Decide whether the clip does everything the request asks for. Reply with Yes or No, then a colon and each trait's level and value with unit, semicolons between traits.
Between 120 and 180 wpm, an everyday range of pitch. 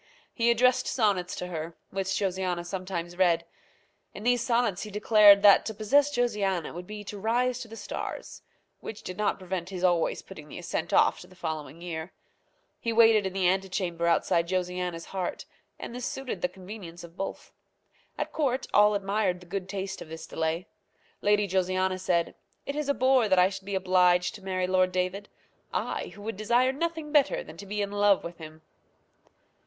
No: average, 190 wpm; average, 3.3 semitones